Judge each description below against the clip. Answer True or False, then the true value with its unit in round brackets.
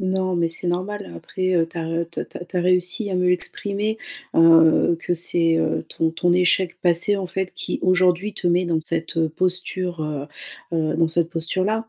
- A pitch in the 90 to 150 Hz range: False (175 Hz)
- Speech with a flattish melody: True (2.0 semitones)